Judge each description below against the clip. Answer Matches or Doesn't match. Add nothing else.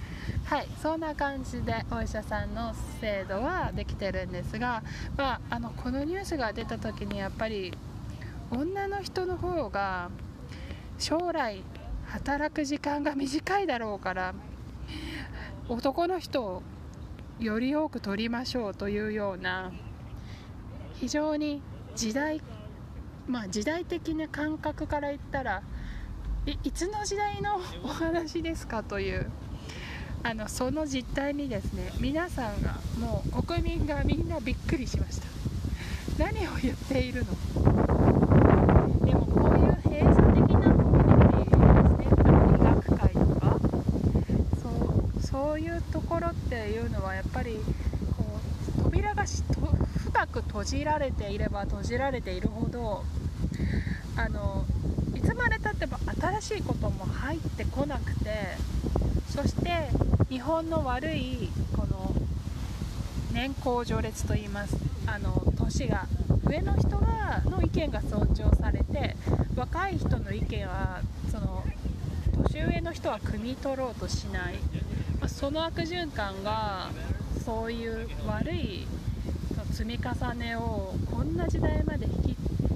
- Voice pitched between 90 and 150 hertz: Doesn't match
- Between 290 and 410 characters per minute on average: Doesn't match